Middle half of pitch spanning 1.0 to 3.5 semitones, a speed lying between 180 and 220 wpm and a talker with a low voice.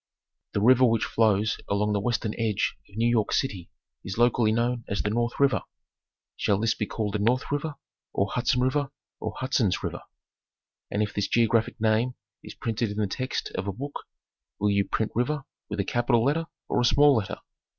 Yes: average, 3.1 semitones; average, 190 wpm; low, 115 Hz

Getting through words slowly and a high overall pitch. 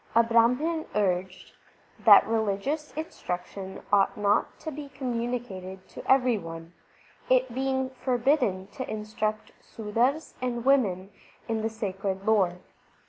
Yes: slow, 120 wpm; high, 225 Hz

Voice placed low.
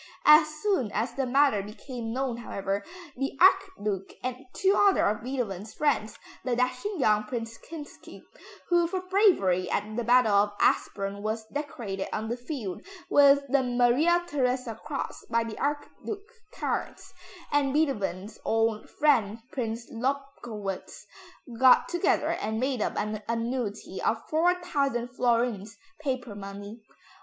No: high, 245 Hz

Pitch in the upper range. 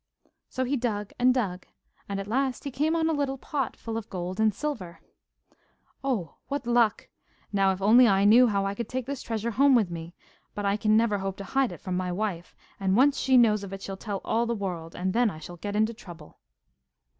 Yes: high, 215 Hz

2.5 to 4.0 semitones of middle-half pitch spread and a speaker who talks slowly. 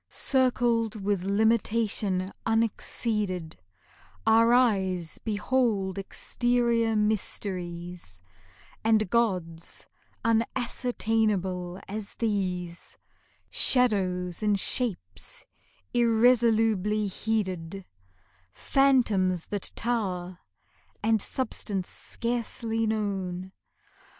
Yes: average, 3.7 semitones; slow, 65 wpm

